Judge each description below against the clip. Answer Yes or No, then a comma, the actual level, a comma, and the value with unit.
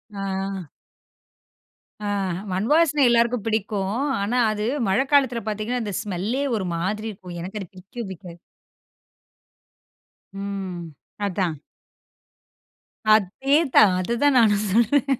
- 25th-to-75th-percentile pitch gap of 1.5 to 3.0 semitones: No, average, 3.8 semitones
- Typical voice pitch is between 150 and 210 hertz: Yes, high, 205 Hz